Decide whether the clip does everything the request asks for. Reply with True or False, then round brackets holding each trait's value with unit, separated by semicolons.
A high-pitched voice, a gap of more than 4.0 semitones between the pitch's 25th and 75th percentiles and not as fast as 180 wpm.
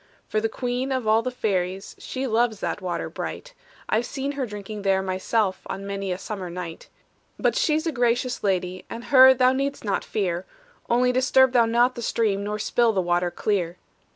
False (220 Hz; 4.7 semitones; 190 wpm)